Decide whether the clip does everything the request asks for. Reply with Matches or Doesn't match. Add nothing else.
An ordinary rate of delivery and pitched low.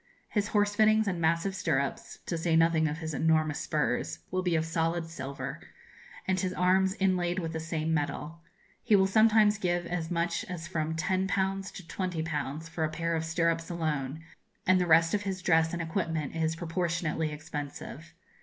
Doesn't match